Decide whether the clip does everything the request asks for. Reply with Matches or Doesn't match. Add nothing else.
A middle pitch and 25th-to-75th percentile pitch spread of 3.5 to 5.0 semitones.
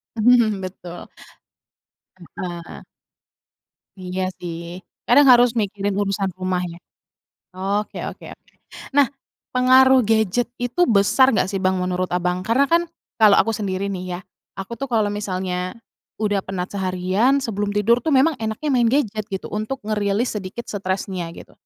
Doesn't match